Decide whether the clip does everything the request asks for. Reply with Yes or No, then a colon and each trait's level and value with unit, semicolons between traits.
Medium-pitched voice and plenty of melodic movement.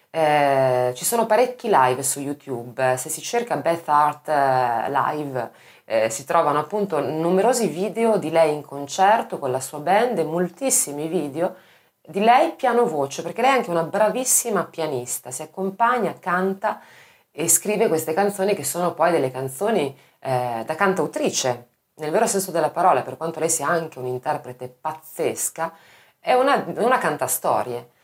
Yes: medium, 160 Hz; wide, 6.3 semitones